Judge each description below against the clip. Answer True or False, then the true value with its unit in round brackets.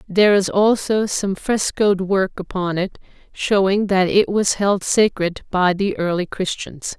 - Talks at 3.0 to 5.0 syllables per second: True (4.1 syllables/s)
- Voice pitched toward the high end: True (195 Hz)